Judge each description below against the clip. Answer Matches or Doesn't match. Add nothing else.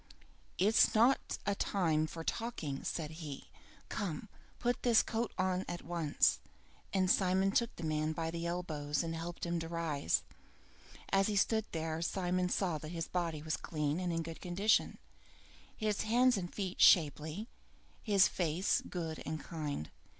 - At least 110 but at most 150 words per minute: Doesn't match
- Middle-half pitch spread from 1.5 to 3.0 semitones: Doesn't match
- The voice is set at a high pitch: Doesn't match